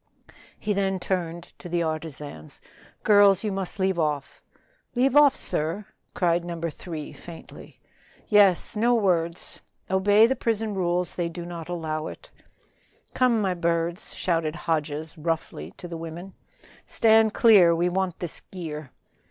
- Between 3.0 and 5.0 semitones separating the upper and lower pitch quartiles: Yes, average, 3.4 semitones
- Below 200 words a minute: Yes, average, 140 wpm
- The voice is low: No, medium, 175 Hz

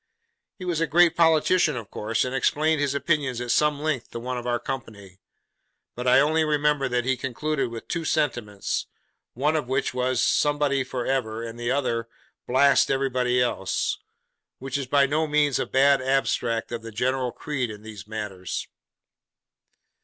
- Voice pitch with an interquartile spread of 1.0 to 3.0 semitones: No, average, 3.6 semitones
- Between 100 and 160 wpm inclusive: No, average, 170 wpm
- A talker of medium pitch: No, low, 130 Hz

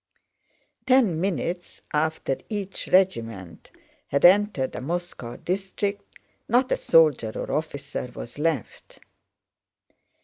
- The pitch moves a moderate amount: No, wide, 6.0 semitones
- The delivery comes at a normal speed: No, slow, 100 wpm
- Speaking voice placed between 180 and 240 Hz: No, medium, 165 Hz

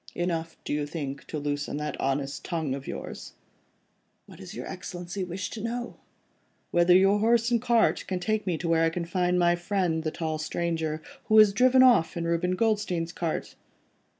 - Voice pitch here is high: No, medium, 175 Hz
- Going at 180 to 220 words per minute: Yes, average, 185 wpm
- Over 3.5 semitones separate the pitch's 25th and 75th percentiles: Yes, average, 4.0 semitones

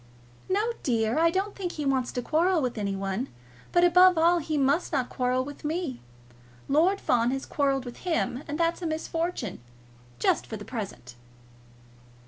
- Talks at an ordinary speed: Yes, average, 170 wpm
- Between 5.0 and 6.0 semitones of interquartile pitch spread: Yes, wide, 5.6 semitones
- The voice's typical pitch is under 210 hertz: No, very high, 290 Hz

